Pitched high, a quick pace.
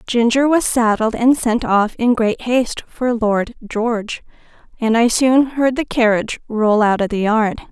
No: high, 230 Hz; average, 180 wpm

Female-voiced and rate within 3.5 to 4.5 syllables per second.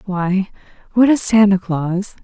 Yes: female; 3.7 syllables/s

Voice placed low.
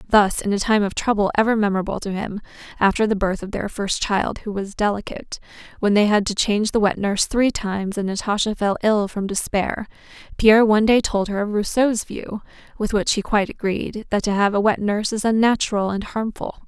No: high, 210 Hz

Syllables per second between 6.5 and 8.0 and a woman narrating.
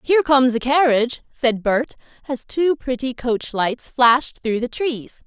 No: 4.5 syllables/s; female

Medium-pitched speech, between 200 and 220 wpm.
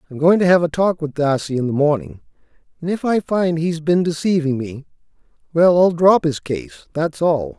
Yes: medium, 165 Hz; fast, 205 wpm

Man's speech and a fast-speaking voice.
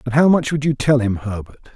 Yes: male; fast, 275 wpm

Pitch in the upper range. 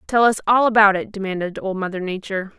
Yes: high, 200 Hz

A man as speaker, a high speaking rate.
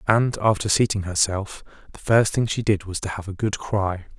Yes: male; fast, 215 wpm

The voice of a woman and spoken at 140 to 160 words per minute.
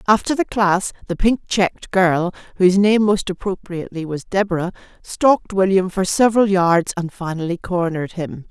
Yes: female; average, 155 wpm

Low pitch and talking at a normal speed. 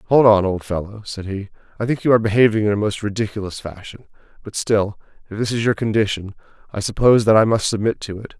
No: low, 105 Hz; fast, 220 wpm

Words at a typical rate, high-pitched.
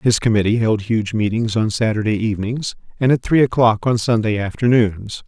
No: average, 170 wpm; low, 110 Hz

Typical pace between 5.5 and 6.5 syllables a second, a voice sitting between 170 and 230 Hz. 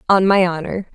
Yes: 5.6 syllables/s; medium, 185 Hz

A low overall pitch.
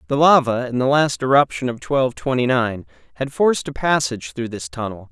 Yes: low, 130 Hz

